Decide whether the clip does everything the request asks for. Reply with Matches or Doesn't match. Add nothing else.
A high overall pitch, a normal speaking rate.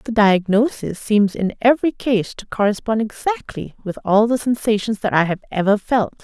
Matches